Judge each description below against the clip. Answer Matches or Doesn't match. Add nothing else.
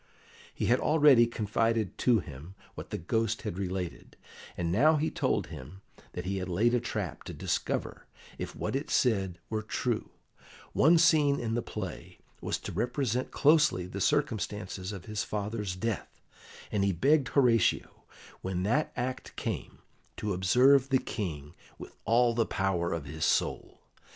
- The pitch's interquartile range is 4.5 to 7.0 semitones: Matches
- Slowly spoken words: Doesn't match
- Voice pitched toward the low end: Matches